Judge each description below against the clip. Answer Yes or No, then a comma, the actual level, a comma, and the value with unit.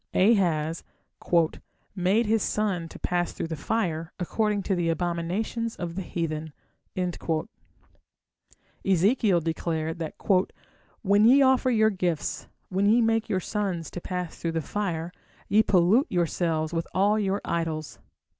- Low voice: No, medium, 180 Hz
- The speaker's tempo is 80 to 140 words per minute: Yes, slow, 135 wpm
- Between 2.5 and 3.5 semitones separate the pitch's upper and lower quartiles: No, average, 4.2 semitones